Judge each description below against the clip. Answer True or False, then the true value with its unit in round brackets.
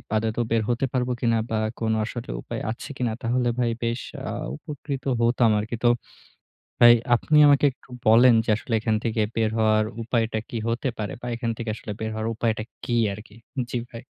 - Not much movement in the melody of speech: True (1.6 semitones)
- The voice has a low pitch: True (115 Hz)